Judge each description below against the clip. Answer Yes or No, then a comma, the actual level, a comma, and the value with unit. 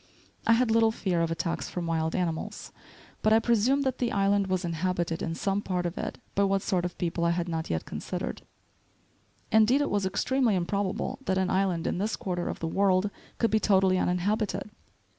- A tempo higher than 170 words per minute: Yes, average, 200 wpm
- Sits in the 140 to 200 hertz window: Yes, high, 190 Hz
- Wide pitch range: No, average, 3.6 semitones